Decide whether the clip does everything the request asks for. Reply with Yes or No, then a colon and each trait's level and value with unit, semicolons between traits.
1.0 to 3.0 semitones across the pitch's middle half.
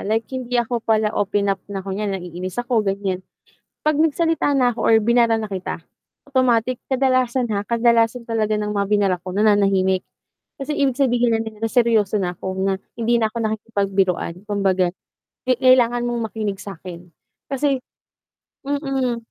No: average, 3.7 semitones